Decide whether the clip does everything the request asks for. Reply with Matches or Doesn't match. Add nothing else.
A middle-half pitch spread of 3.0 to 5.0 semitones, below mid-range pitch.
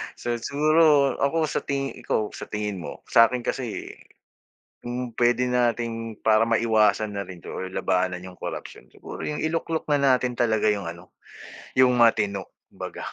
Matches